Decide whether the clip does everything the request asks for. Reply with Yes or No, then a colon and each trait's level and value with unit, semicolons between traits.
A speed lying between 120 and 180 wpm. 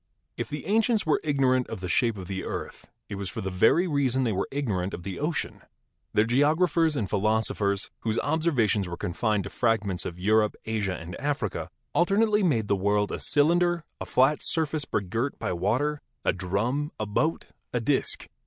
No: average, 190 wpm